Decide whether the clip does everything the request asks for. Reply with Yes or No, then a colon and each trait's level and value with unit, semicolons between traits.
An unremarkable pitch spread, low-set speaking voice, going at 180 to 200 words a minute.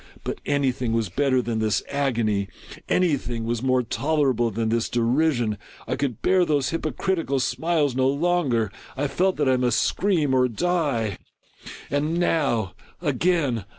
No: average, 4.9 semitones; low, 130 Hz; average, 165 wpm